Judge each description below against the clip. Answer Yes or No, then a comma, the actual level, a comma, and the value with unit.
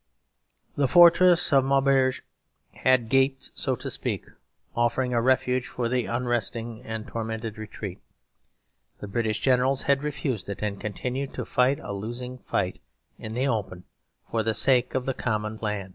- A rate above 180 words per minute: No, average, 155 wpm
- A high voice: No, low, 120 Hz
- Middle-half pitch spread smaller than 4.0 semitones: Yes, average, 3.3 semitones